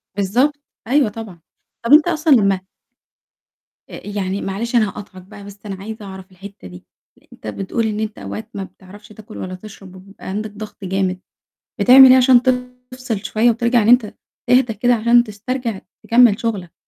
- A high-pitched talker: Yes, high, 215 Hz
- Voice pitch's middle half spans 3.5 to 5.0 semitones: Yes, average, 3.8 semitones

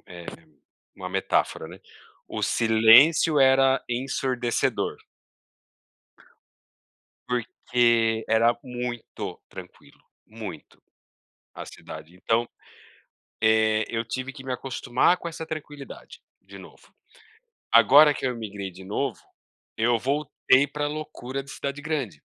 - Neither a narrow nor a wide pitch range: Yes, average, 3.7 semitones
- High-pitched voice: No, low, 125 Hz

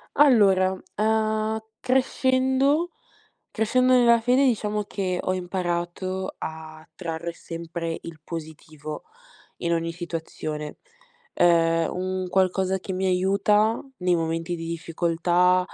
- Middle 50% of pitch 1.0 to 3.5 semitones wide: No, average, 4.4 semitones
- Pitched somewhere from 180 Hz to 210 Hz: Yes, medium, 185 Hz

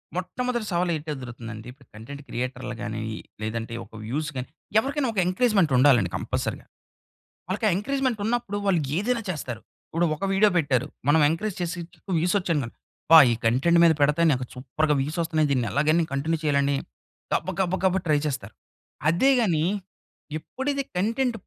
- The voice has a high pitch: No, medium, 160 Hz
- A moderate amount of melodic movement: No, wide, 6.5 semitones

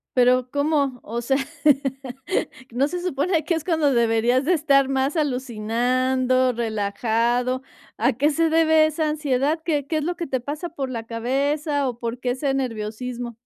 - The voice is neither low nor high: No, very high, 265 Hz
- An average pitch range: Yes, average, 3.6 semitones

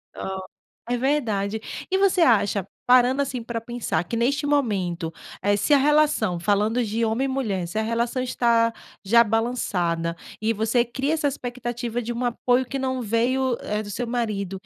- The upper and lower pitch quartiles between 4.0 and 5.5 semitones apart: No, average, 3.5 semitones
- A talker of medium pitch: No, high, 235 Hz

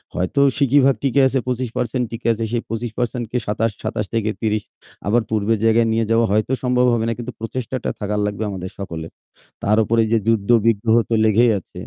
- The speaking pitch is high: No, low, 115 Hz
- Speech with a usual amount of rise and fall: No, narrow, 2.3 semitones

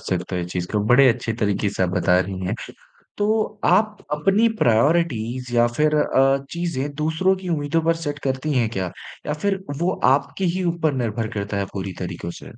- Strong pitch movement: Yes, wide, 8.3 semitones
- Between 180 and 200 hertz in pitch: No, low, 135 Hz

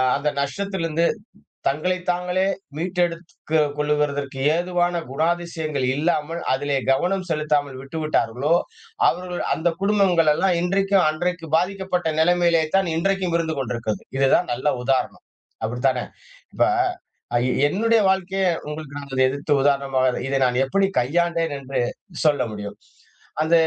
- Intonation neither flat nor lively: Yes, average, 4.1 semitones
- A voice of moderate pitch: Yes, medium, 160 Hz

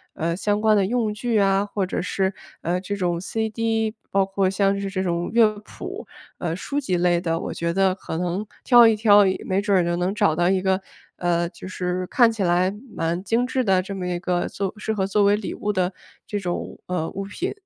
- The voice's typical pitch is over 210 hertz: No, high, 195 Hz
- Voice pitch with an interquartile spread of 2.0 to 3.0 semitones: Yes, average, 2.7 semitones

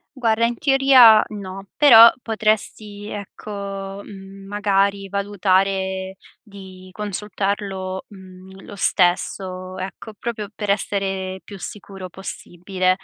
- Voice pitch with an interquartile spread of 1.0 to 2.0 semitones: Yes, narrow, 1.7 semitones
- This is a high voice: Yes, high, 195 Hz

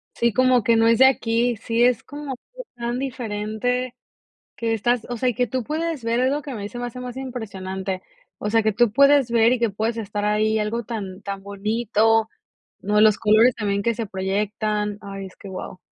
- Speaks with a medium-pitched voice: No, high, 225 Hz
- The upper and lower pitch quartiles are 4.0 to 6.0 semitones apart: No, average, 2.9 semitones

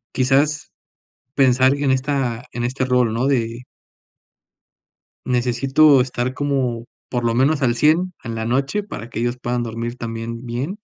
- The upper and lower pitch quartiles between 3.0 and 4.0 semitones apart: No, narrow, 2.5 semitones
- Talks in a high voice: No, low, 125 Hz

